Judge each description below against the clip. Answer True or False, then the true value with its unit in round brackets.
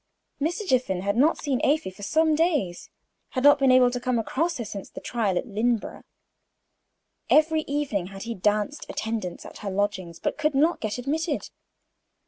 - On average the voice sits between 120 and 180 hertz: False (245 Hz)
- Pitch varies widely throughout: True (6.6 semitones)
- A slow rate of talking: False (175 wpm)